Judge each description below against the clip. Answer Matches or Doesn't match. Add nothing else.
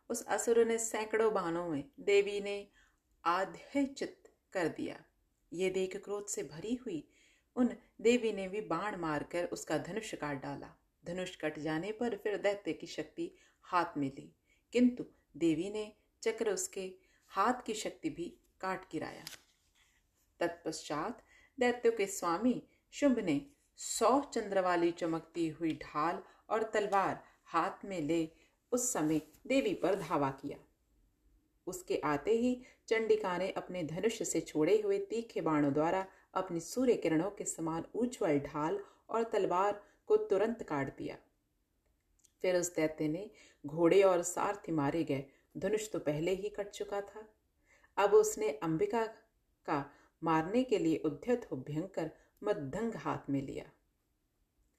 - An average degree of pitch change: Doesn't match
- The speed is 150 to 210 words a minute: Doesn't match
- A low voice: Doesn't match